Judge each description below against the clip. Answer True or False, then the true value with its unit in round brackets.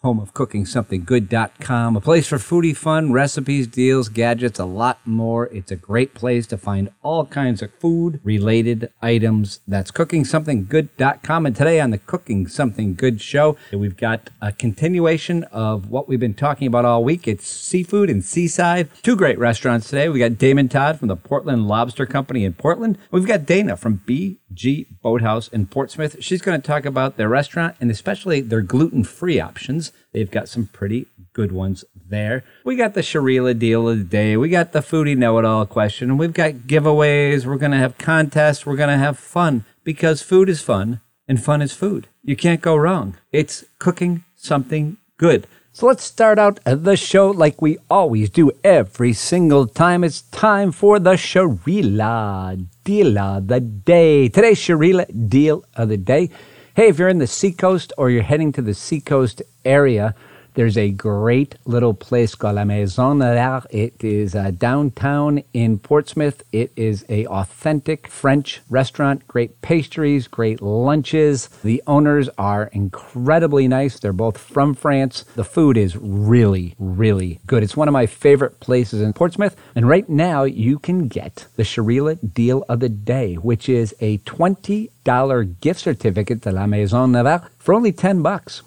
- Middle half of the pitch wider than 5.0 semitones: True (5.5 semitones)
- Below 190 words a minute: True (175 wpm)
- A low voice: True (130 Hz)